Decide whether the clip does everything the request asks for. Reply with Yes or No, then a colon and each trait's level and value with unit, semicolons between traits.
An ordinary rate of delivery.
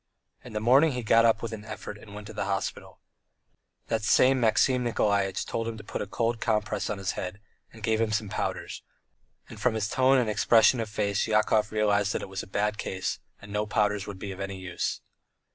No: fast, 220 wpm